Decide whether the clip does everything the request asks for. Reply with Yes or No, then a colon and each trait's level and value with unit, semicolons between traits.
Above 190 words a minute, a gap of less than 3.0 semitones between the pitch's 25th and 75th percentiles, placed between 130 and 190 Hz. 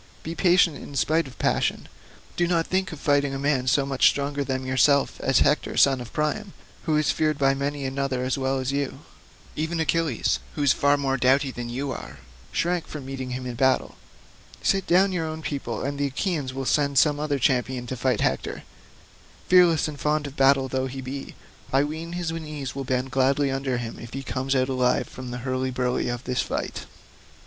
Yes: fast, 205 wpm; narrow, 2.6 semitones; medium, 140 Hz